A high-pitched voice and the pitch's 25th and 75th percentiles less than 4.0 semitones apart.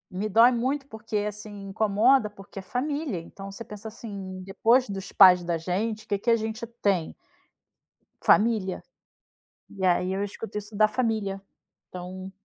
Yes: high, 210 Hz; average, 2.8 semitones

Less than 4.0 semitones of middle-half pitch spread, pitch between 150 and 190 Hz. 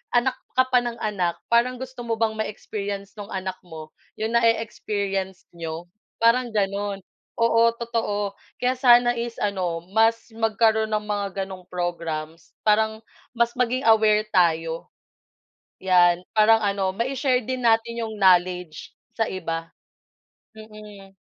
No: average, 3.6 semitones; high, 215 Hz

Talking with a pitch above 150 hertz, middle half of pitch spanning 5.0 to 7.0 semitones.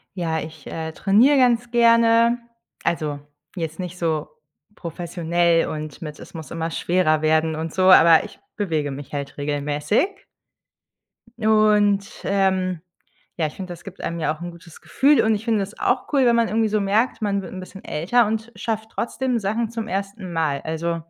Yes: medium, 185 Hz; wide, 5.4 semitones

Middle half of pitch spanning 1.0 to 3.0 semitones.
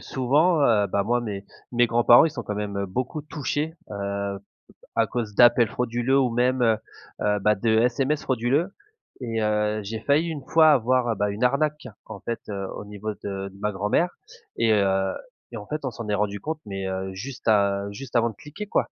No: average, 4.3 semitones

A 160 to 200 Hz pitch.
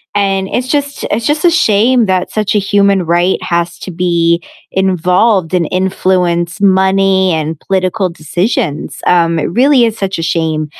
Yes: high, 190 Hz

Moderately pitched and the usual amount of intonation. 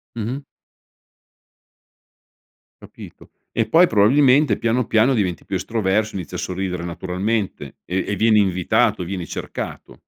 No: low, 105 Hz; average, 3.7 semitones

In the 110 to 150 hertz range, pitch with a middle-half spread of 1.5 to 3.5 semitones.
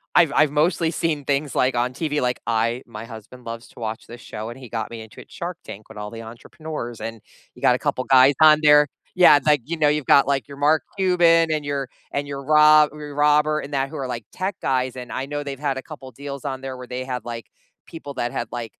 No: medium, 140 Hz; average, 3.9 semitones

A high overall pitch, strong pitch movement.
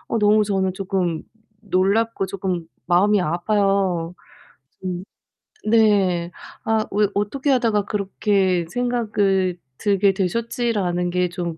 No: high, 195 Hz; average, 2.8 semitones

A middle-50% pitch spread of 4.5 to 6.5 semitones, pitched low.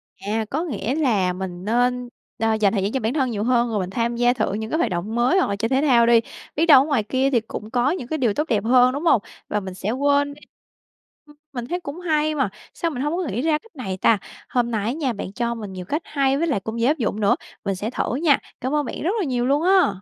No: average, 4.9 semitones; high, 245 Hz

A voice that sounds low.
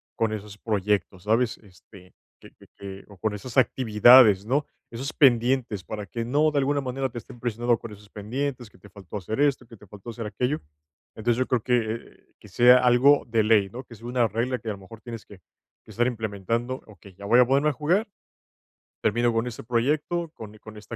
Yes: low, 115 Hz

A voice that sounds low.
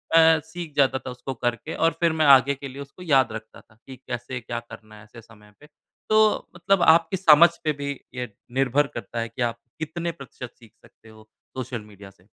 Yes: low, 130 Hz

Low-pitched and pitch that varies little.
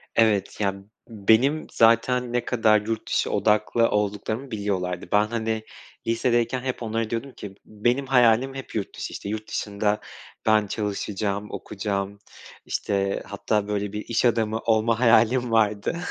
Yes: low, 110 Hz; narrow, 2.2 semitones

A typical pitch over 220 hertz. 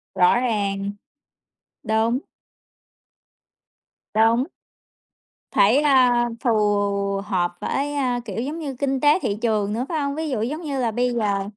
Yes: high, 240 Hz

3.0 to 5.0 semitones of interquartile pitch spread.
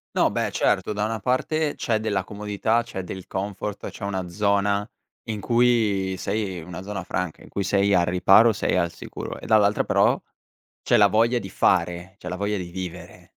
No: narrow, 2.6 semitones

